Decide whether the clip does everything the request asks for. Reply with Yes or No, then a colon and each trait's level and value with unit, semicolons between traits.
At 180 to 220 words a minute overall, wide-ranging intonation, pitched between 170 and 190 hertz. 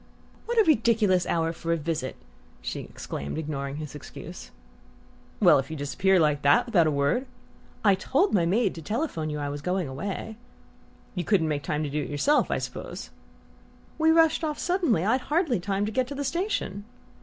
Yes: average, 190 wpm; wide, 8.9 semitones; medium, 185 Hz